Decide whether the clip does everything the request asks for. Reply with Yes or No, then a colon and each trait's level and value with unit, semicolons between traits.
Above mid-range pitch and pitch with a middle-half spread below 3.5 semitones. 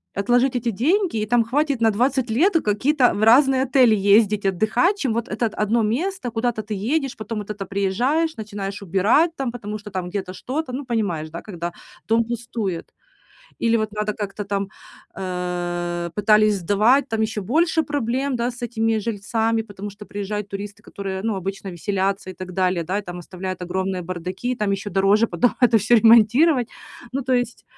No: high, 215 Hz; average, 3.8 semitones